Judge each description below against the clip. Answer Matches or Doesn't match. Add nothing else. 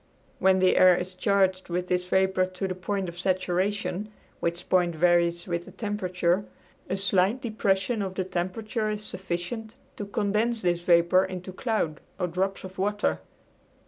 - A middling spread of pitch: Doesn't match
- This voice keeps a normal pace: Matches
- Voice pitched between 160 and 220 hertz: Matches